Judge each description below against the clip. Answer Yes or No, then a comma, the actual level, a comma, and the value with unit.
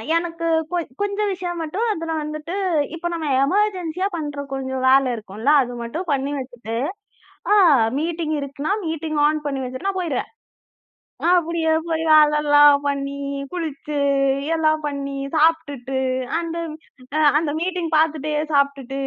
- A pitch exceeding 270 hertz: Yes, very high, 310 Hz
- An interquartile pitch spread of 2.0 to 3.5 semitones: Yes, average, 3.1 semitones